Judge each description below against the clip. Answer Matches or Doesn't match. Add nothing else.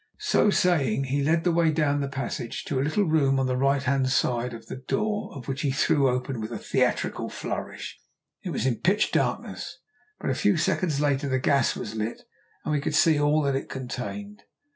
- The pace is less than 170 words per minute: Doesn't match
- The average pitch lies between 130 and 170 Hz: Matches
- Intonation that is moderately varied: Matches